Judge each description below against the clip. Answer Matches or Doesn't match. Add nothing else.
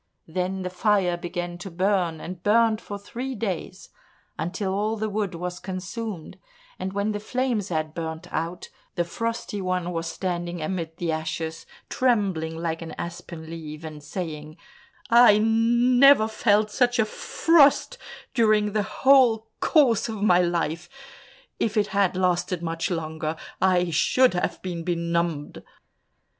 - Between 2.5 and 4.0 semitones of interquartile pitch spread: Doesn't match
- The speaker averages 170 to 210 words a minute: Doesn't match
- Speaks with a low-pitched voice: Doesn't match